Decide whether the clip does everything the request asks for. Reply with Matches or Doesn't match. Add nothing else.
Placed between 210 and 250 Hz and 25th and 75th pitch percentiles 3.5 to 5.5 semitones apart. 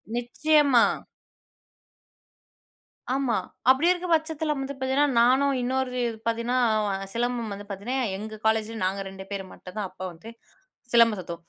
Matches